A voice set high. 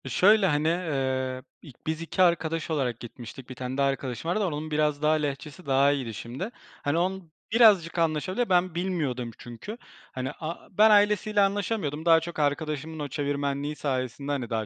No: medium, 150 Hz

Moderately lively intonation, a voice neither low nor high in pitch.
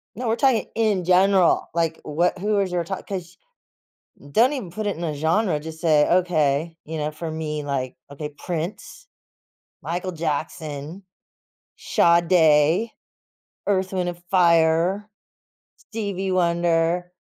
Yes: average, 3.2 semitones; medium, 170 Hz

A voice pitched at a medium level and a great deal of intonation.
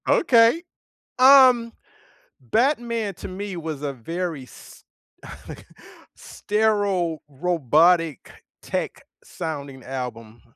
Yes: medium, 175 Hz; wide, 7.7 semitones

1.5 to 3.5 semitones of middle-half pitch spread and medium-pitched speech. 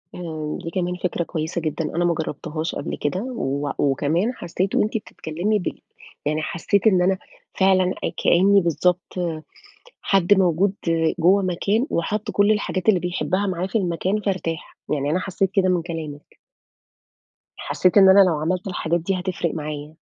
Yes: average, 2.9 semitones; medium, 180 Hz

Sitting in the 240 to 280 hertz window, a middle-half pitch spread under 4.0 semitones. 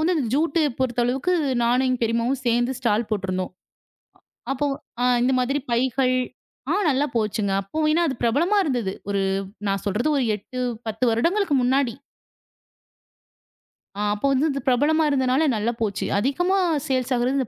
Yes: very high, 255 Hz; average, 3.4 semitones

